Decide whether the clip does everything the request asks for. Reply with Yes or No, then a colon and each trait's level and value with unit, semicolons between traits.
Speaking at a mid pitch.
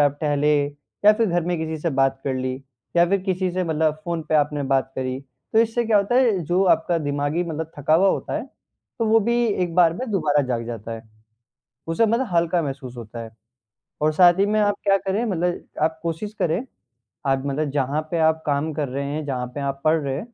Yes: medium, 160 Hz